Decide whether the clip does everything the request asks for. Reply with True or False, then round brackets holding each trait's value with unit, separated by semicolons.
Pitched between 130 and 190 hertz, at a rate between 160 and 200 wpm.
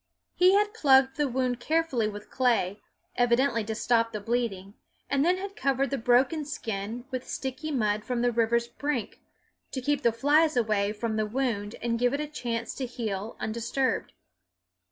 False (245 Hz; 175 wpm)